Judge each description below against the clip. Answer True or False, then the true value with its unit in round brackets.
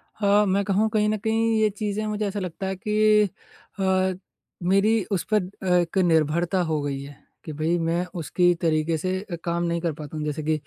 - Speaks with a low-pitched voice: False (185 Hz)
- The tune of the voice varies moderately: True (4.2 semitones)